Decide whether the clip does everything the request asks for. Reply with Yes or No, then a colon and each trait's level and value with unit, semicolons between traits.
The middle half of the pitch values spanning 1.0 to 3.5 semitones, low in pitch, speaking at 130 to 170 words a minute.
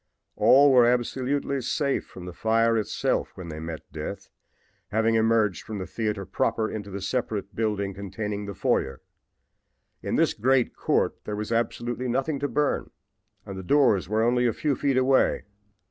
No: average, 4.1 semitones; low, 115 Hz; average, 165 wpm